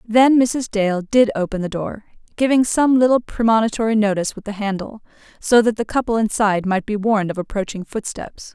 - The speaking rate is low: No, average, 185 wpm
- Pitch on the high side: Yes, high, 215 Hz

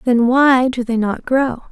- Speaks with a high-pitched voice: Yes, very high, 250 Hz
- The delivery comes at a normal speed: No, fast, 210 wpm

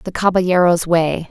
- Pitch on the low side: No, medium, 175 Hz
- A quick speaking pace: No, average, 140 wpm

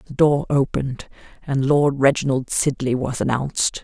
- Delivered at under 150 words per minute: Yes, average, 140 wpm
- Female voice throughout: Yes, female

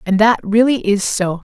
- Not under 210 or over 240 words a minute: No, average, 200 wpm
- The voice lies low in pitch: No, high, 210 Hz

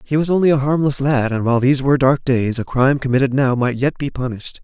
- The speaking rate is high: Yes, fast, 260 wpm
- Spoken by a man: Yes, male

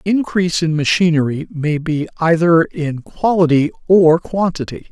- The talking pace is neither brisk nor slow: No, slow, 120 wpm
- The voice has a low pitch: No, medium, 165 Hz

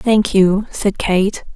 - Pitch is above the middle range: Yes, high, 200 Hz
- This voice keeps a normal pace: Yes, average, 155 wpm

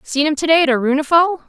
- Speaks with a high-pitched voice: Yes, very high, 300 Hz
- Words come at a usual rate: No, fast, 245 wpm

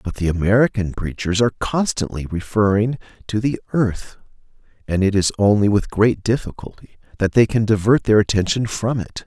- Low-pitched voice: Yes, low, 105 Hz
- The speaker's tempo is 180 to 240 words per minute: No, average, 160 wpm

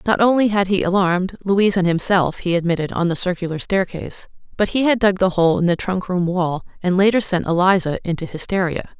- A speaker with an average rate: Yes, average, 195 wpm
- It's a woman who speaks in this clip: Yes, female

